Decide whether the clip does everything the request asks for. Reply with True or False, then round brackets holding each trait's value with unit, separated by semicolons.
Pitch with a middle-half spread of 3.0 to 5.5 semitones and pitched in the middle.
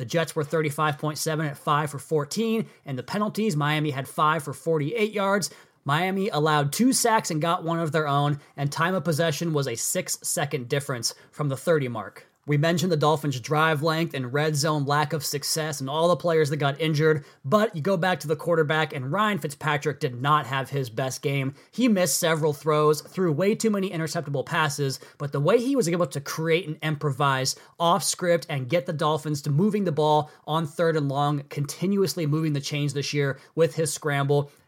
False (2.6 semitones; 155 Hz)